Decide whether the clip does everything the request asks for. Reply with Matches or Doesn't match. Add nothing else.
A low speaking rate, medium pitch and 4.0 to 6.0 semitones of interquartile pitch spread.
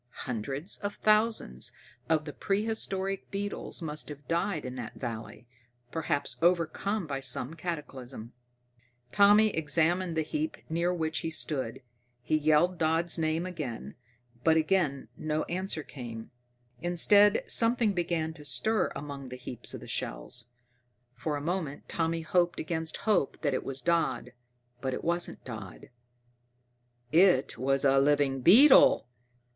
Matches